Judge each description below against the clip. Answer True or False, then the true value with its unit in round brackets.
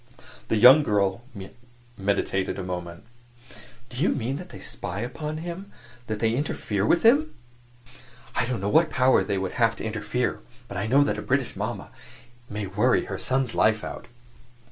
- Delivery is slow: False (165 wpm)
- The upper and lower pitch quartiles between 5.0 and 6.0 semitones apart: True (5.5 semitones)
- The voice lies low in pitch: True (115 Hz)